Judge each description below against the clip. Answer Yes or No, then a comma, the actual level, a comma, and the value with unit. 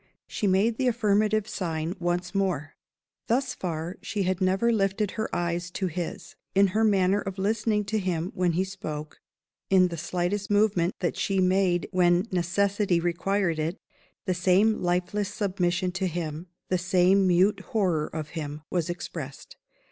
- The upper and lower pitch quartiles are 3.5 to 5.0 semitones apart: No, narrow, 2.5 semitones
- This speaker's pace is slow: No, average, 155 wpm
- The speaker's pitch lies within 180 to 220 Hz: Yes, medium, 185 Hz